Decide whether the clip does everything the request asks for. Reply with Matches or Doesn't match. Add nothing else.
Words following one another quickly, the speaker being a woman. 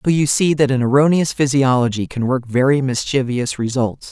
Doesn't match